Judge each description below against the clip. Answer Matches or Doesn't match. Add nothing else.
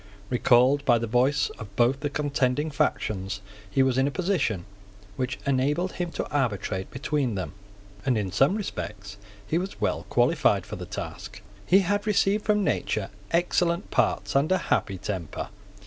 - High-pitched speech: Doesn't match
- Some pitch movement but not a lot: Doesn't match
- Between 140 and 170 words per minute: Matches